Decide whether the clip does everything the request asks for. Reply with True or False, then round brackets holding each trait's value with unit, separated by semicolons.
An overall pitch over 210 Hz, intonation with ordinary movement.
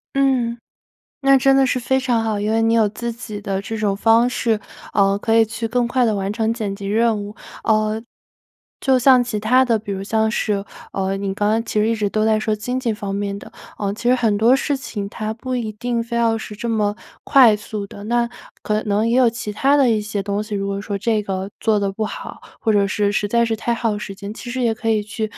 False (220 Hz; 2.3 semitones)